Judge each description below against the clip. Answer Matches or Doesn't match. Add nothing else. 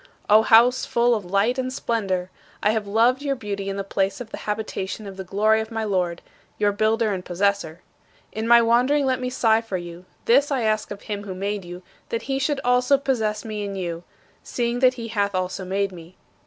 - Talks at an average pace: Doesn't match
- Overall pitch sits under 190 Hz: Doesn't match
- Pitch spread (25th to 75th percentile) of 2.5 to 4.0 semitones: Matches